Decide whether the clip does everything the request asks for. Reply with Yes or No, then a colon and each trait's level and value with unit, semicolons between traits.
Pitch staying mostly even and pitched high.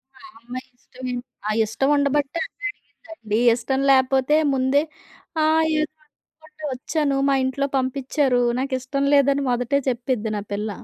Yes: narrow, 2.2 semitones; very high, 265 Hz